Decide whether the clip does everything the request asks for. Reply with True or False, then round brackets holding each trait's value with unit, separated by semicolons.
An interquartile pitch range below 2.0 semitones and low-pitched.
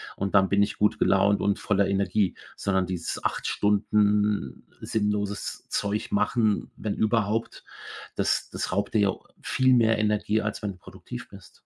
True (1.2 semitones; 105 Hz)